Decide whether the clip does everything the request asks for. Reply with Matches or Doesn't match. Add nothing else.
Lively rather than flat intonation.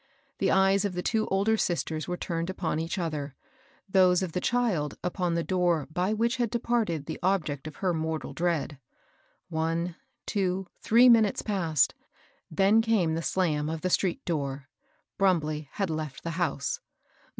Doesn't match